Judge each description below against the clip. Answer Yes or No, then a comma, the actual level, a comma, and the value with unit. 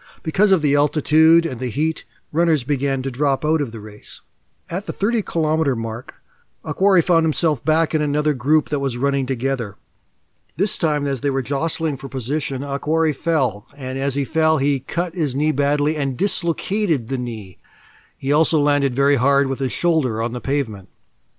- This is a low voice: No, medium, 145 Hz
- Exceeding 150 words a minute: Yes, average, 180 wpm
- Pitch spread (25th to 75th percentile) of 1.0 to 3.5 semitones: Yes, average, 2.9 semitones